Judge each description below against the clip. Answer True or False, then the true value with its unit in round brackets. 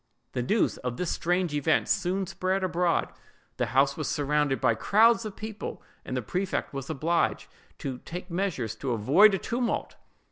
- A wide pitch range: True (6.4 semitones)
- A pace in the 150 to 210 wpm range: True (170 wpm)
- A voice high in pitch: False (170 Hz)